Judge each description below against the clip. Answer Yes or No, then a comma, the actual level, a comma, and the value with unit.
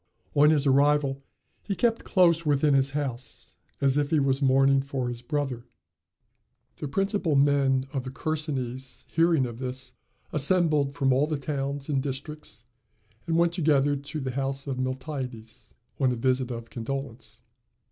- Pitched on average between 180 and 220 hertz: No, medium, 140 Hz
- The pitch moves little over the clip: Yes, narrow, 2.3 semitones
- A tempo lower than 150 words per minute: No, average, 155 wpm